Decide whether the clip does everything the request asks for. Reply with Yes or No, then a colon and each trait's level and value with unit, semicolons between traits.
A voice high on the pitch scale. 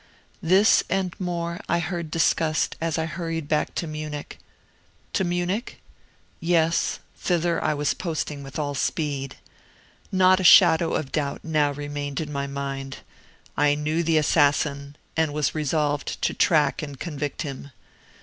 No: medium, 155 Hz